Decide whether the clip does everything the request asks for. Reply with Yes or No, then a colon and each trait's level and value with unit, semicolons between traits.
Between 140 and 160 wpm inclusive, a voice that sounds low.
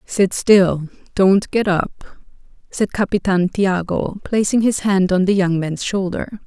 No: average, 150 wpm; high, 190 Hz